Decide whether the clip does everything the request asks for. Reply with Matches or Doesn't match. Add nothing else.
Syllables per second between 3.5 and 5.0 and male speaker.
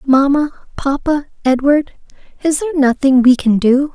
Doesn't match